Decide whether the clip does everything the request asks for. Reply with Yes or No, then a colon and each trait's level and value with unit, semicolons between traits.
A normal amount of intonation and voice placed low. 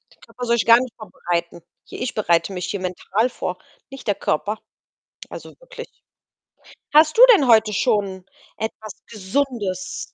No: average, 4.8 semitones; high, 215 Hz